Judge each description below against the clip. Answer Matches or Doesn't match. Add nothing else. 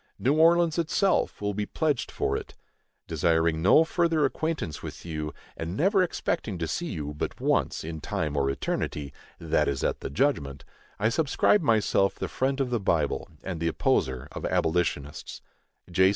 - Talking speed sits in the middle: Matches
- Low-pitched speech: Matches